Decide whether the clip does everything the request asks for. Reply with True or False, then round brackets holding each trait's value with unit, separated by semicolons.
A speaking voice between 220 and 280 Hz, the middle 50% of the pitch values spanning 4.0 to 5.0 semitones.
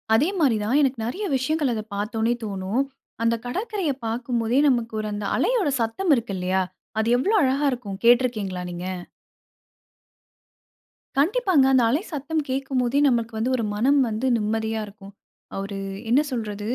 True (240 Hz; 4.4 semitones)